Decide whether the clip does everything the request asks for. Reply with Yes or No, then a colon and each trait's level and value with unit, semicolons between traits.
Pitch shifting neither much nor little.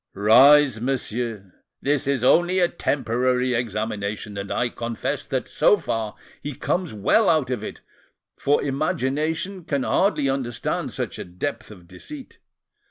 Yes: average, 4.9 semitones